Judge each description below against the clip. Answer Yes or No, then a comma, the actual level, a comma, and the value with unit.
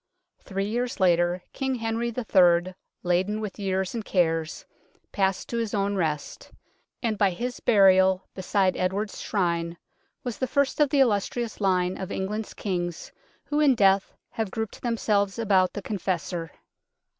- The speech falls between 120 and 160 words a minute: Yes, average, 145 wpm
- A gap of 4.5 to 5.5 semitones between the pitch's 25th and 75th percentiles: No, average, 3.5 semitones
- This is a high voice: Yes, high, 195 Hz